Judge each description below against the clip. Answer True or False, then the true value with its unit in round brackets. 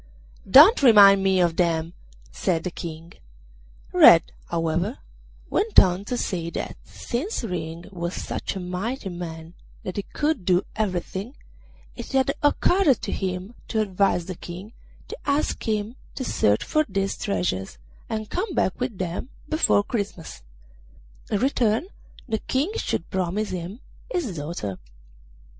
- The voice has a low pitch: False (195 Hz)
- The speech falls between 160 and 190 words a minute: False (140 wpm)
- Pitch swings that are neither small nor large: False (5.9 semitones)